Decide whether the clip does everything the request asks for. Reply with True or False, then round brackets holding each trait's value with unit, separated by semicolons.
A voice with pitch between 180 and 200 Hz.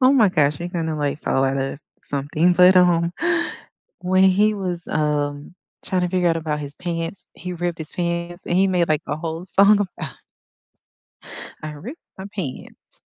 False (170 Hz)